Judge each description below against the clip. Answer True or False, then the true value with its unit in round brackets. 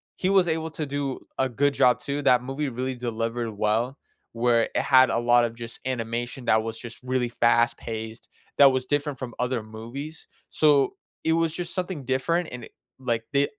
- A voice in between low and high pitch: False (125 Hz)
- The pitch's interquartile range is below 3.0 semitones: False (3.4 semitones)